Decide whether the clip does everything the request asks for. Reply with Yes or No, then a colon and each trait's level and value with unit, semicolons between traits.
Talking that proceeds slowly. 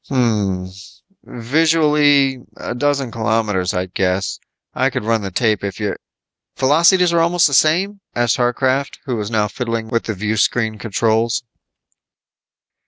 No: average, 145 wpm